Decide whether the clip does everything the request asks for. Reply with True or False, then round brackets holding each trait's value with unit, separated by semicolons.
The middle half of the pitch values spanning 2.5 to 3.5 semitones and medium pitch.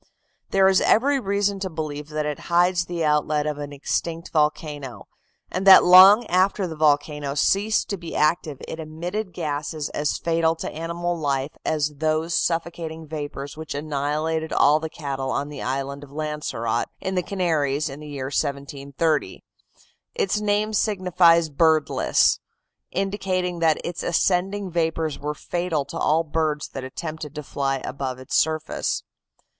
True (3.2 semitones; 160 Hz)